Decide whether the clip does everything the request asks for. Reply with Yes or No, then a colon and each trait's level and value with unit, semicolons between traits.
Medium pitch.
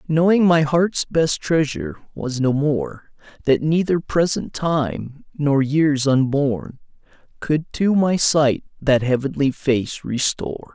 Yes: medium, 145 Hz